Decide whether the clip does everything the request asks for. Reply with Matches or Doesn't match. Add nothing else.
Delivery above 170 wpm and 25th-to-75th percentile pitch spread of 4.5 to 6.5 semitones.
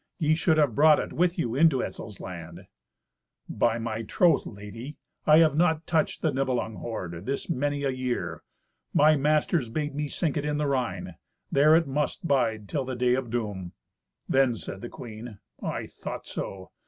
Matches